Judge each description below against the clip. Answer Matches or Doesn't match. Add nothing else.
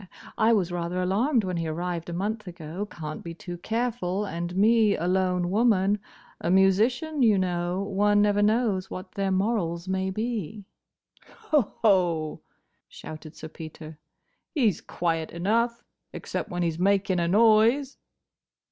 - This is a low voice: Doesn't match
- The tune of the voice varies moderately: Matches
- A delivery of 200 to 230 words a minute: Doesn't match